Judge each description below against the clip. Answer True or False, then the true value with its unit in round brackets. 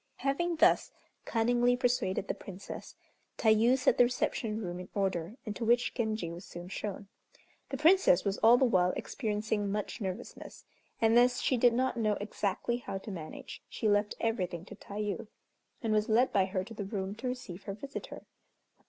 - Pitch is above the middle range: True (215 Hz)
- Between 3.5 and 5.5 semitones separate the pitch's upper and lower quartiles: True (3.8 semitones)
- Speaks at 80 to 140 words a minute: False (175 wpm)